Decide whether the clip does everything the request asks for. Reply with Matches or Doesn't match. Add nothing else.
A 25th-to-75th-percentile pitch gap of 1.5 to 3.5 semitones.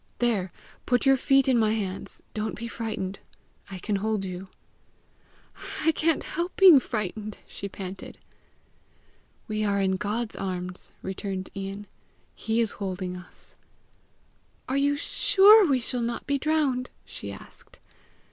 Doesn't match